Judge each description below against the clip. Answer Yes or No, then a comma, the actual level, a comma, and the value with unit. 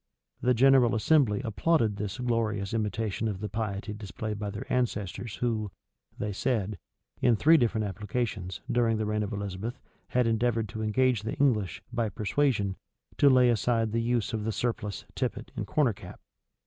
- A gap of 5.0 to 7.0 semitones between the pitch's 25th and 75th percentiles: No, average, 2.8 semitones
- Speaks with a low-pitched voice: Yes, low, 110 Hz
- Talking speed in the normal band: Yes, average, 165 wpm